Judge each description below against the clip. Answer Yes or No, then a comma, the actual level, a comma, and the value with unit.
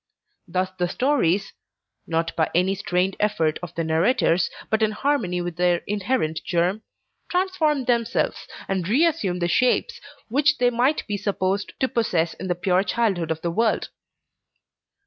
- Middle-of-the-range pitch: No, high, 195 Hz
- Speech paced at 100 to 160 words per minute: Yes, average, 155 wpm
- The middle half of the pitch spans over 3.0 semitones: Yes, wide, 5.6 semitones